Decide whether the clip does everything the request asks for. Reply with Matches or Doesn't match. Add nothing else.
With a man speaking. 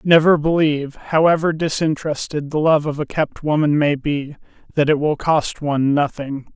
Matches